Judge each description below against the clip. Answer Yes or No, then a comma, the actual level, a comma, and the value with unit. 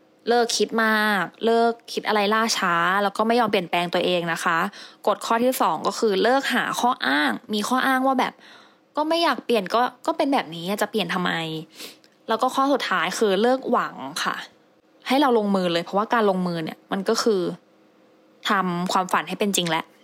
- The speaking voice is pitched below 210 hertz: No, high, 215 Hz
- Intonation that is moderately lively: Yes, average, 4.3 semitones